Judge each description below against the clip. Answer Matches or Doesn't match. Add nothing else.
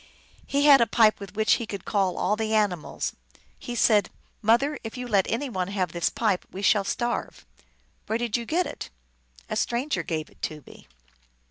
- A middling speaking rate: Doesn't match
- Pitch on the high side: Matches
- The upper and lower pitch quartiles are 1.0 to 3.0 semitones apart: Doesn't match